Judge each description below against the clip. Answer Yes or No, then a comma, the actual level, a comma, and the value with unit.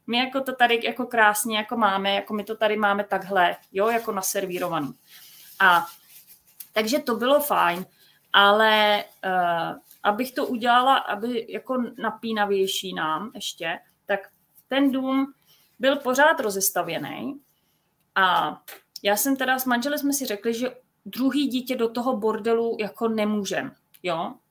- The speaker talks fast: No, average, 135 wpm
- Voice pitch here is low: No, high, 220 Hz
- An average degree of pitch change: Yes, average, 4.2 semitones